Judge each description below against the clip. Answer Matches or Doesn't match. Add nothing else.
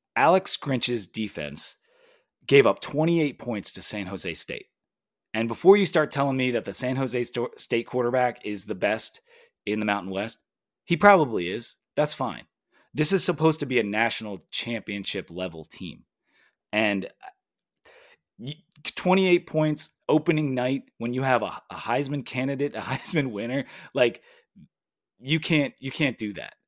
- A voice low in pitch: Matches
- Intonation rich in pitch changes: Matches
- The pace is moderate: Matches